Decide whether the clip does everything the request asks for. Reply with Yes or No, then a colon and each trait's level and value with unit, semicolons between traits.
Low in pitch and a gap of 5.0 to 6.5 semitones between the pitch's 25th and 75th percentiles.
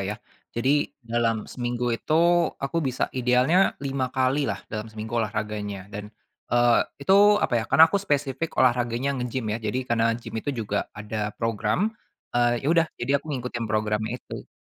No: low, 120 Hz; average, 3.8 semitones